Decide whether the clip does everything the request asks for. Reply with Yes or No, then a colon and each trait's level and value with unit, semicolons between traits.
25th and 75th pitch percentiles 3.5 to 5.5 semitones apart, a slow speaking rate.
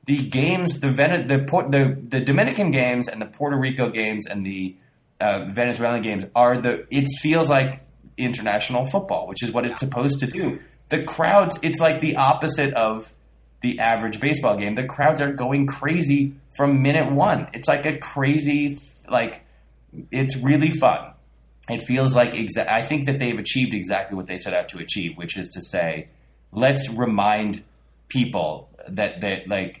No: average, 4.7 semitones; average, 175 wpm